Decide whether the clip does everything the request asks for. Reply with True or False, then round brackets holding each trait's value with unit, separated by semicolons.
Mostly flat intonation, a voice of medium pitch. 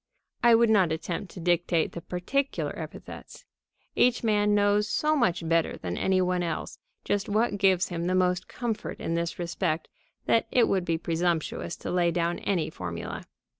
False (3.5 semitones; 180 Hz)